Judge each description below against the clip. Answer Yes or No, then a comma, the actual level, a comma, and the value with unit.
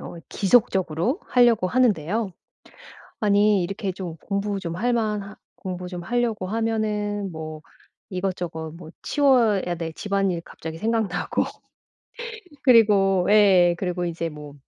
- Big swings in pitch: No, average, 3.6 semitones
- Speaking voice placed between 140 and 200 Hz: Yes, high, 195 Hz